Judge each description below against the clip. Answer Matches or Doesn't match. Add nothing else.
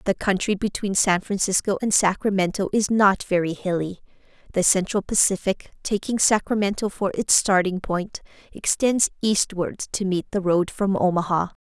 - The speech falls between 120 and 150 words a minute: Matches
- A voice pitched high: Matches